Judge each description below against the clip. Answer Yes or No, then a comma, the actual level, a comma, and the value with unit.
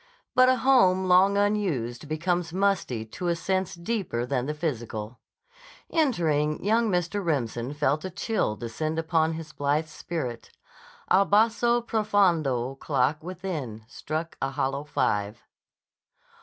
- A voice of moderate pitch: Yes, medium, 160 Hz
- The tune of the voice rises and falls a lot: Yes, wide, 6.3 semitones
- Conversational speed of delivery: No, slow, 130 wpm